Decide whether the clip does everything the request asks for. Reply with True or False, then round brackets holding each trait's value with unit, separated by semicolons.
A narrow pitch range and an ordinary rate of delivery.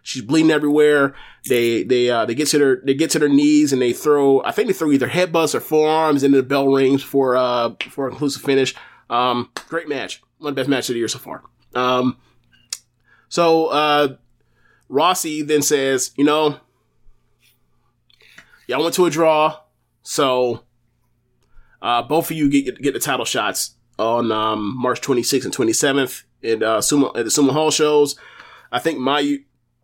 False (3.4 semitones; 180 wpm)